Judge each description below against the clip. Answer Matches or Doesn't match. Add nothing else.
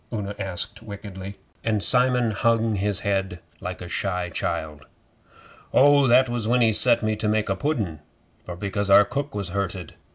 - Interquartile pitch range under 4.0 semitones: Matches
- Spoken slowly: Doesn't match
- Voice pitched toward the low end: Matches